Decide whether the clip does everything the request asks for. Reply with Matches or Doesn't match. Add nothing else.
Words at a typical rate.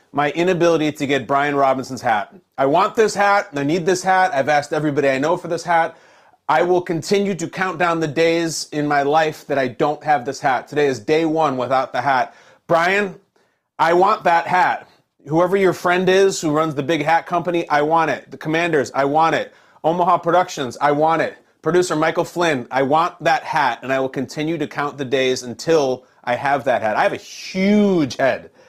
Doesn't match